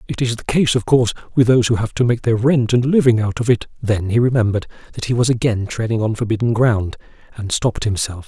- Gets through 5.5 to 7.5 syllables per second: Yes, 6.4 syllables/s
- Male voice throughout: Yes, male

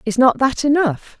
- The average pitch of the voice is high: Yes, very high, 250 Hz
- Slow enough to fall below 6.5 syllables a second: Yes, 4.7 syllables/s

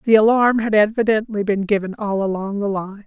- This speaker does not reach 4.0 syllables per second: No, 5.4 syllables/s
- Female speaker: Yes, female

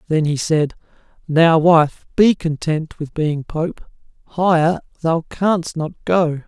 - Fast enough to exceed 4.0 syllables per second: No, 3.5 syllables/s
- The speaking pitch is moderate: Yes, medium, 160 Hz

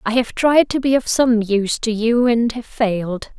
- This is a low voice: No, high, 230 Hz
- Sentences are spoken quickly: Yes, fast, 230 wpm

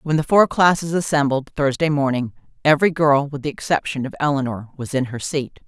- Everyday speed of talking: Yes, average, 190 wpm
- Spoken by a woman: Yes, female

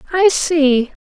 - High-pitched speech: Yes, very high, 310 Hz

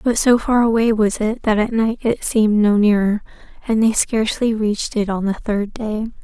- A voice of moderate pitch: No, high, 220 Hz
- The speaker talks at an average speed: No, fast, 210 wpm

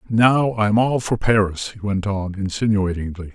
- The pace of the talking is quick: No, average, 160 wpm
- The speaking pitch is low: Yes, low, 105 Hz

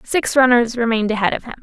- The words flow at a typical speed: No, fast, 220 wpm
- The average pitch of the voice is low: No, high, 235 Hz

